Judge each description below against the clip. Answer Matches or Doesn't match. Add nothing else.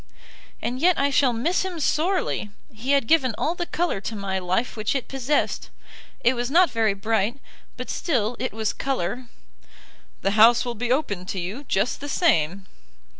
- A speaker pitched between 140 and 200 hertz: Doesn't match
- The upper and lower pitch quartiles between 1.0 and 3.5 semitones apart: Doesn't match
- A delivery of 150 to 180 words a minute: Matches